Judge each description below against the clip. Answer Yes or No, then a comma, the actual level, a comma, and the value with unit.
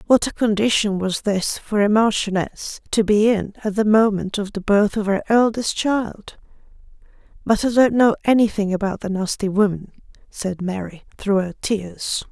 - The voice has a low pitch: No, high, 205 Hz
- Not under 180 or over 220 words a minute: No, average, 170 wpm